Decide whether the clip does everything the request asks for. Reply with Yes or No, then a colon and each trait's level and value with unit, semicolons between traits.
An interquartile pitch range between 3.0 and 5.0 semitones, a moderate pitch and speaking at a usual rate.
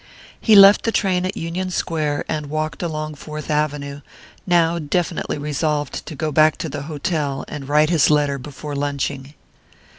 No: narrow, 2.5 semitones; medium, 150 Hz; average, 160 wpm